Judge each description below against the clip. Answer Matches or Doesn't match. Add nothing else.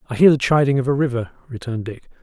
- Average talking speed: Doesn't match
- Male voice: Matches